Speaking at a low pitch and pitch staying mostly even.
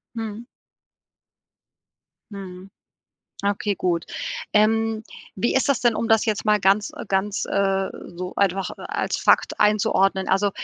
No: high, 200 Hz; narrow, 2.3 semitones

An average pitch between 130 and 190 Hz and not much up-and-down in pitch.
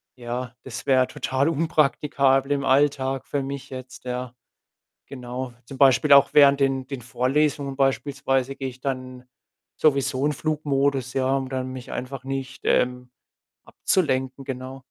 Yes: low, 135 Hz; narrow, 1.4 semitones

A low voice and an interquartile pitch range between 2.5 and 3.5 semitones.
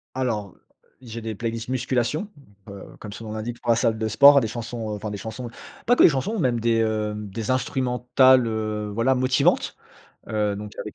Yes: low, 115 Hz; average, 2.9 semitones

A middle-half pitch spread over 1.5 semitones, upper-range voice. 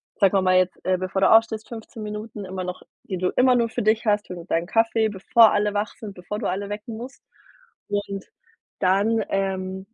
Yes: average, 2.8 semitones; high, 205 Hz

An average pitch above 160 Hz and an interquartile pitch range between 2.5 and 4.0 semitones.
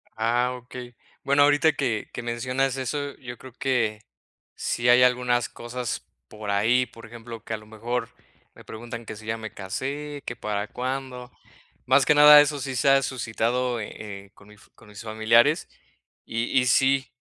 No: low, 120 Hz; average, 2.8 semitones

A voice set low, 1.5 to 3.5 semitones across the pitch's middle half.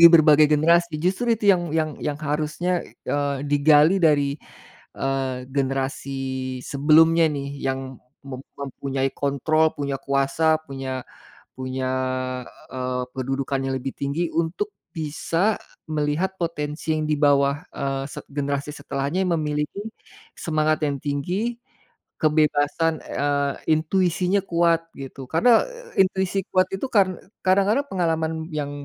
No: medium, 150 Hz; average, 3.2 semitones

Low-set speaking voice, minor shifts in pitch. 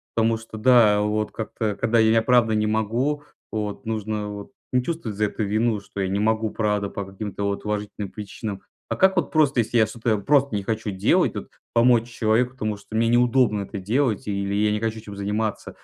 Yes: low, 110 Hz; narrow, 2.1 semitones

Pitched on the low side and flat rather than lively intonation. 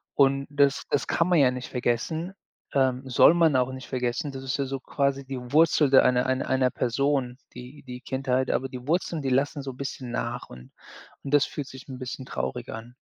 Yes: low, 130 Hz; narrow, 1.8 semitones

